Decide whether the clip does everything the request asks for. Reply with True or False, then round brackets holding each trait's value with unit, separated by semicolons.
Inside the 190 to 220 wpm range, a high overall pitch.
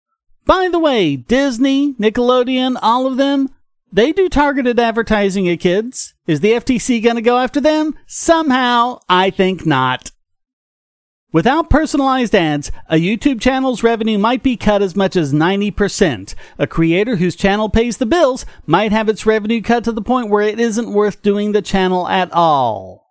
False (165 wpm; 230 Hz)